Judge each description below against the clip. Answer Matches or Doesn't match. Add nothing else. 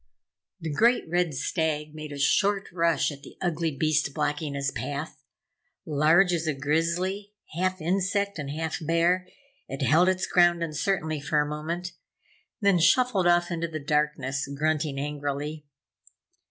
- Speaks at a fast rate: Doesn't match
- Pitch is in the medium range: Matches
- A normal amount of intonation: Matches